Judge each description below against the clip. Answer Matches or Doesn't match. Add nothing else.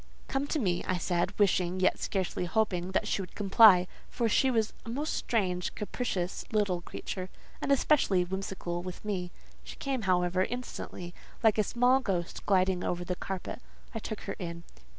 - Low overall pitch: Doesn't match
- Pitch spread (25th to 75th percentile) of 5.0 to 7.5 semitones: Doesn't match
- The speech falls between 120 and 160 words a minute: Doesn't match